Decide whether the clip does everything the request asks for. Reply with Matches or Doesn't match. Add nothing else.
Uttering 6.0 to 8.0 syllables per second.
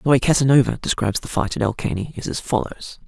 Matches